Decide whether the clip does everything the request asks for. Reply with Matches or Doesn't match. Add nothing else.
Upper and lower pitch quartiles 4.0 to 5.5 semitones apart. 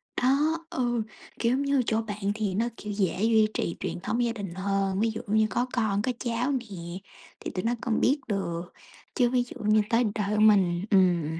Doesn't match